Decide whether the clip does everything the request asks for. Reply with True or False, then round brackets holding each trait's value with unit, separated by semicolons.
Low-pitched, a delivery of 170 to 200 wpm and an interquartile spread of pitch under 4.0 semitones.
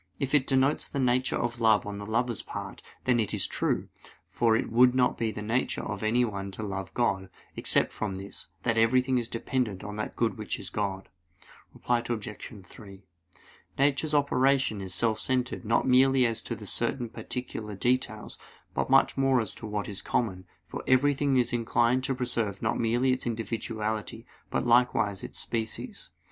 True (115 Hz; 180 wpm; 3.2 semitones)